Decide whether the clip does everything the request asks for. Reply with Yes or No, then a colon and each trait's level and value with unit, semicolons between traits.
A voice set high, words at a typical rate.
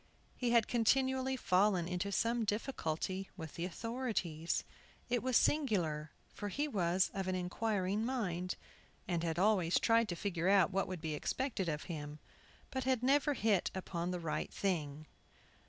Yes: high, 195 Hz; average, 155 wpm